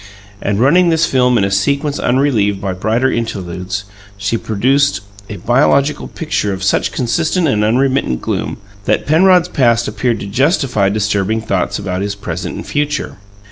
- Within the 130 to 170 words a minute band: Yes, average, 155 wpm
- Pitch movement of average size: No, wide, 5.9 semitones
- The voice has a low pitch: Yes, low, 115 Hz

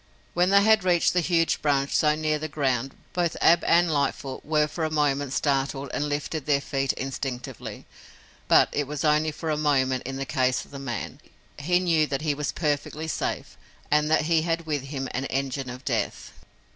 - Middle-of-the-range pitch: Yes, medium, 150 Hz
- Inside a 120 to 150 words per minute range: No, average, 195 wpm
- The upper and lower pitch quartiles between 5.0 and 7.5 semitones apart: No, narrow, 2.6 semitones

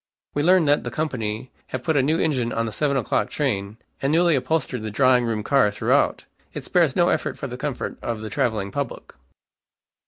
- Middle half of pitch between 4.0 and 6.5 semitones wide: Yes, average, 5.0 semitones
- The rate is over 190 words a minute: Yes, average, 200 wpm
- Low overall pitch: Yes, low, 130 Hz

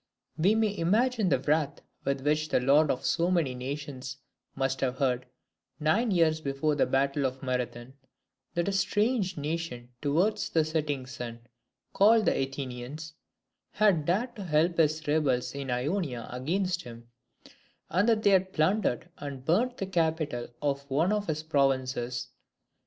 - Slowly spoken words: No, average, 150 wpm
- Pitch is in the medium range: Yes, medium, 150 Hz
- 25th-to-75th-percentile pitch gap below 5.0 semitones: No, wide, 5.4 semitones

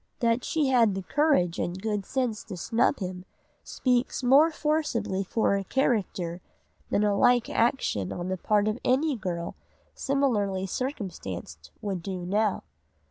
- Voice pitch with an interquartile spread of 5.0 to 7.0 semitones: Yes, wide, 5.4 semitones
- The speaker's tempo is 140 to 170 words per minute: Yes, average, 150 wpm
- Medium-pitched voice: No, high, 210 Hz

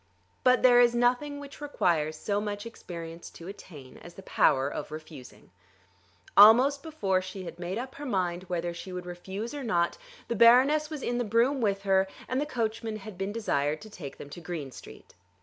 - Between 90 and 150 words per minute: No, average, 195 wpm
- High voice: Yes, high, 200 Hz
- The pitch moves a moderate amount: No, wide, 5.8 semitones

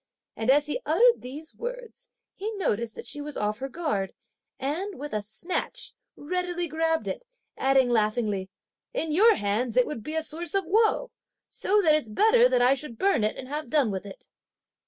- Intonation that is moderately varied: No, wide, 7.5 semitones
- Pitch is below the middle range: No, very high, 300 Hz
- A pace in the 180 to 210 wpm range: Yes, average, 190 wpm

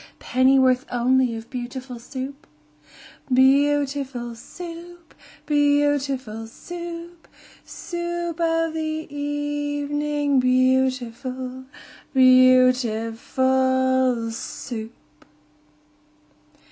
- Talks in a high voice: Yes, very high, 265 Hz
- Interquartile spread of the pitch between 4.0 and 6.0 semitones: No, narrow, 2.5 semitones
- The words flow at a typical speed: No, slow, 85 wpm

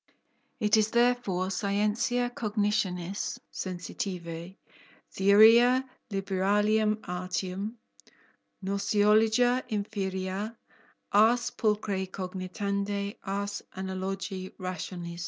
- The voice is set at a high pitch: Yes, high, 200 Hz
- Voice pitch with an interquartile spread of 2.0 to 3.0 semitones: Yes, narrow, 2.4 semitones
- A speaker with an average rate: No, slow, 65 wpm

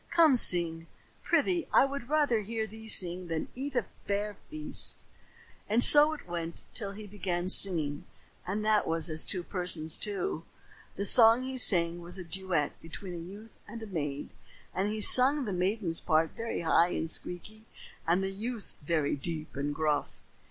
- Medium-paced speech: Yes, average, 175 wpm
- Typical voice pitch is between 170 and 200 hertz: Yes, high, 190 Hz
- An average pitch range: Yes, average, 5.0 semitones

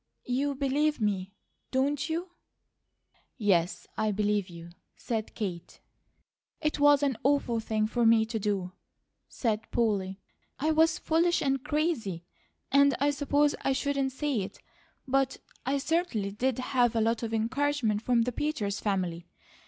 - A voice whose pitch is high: Yes, high, 245 Hz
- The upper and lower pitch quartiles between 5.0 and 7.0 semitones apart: Yes, average, 5.3 semitones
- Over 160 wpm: No, average, 145 wpm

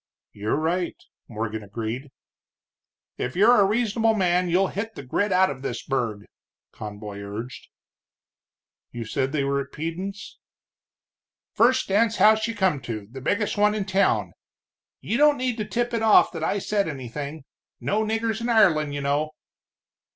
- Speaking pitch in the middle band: Yes, medium, 180 Hz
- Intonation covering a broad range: Yes, wide, 8.5 semitones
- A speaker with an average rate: Yes, average, 160 wpm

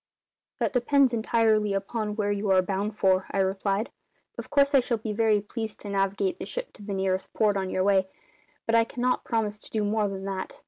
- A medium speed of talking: No, fast, 215 wpm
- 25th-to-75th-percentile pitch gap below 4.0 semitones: Yes, average, 2.7 semitones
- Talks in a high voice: Yes, high, 210 Hz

